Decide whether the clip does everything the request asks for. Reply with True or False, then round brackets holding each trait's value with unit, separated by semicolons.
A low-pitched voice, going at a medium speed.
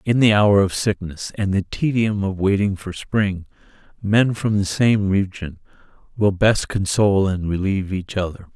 True (100 Hz; 170 wpm)